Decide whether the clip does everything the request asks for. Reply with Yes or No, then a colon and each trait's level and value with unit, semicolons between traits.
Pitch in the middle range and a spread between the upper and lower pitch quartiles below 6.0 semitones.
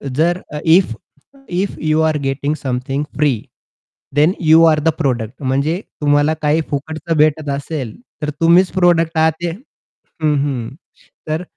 Yes: medium, 155 Hz; narrow, 2.6 semitones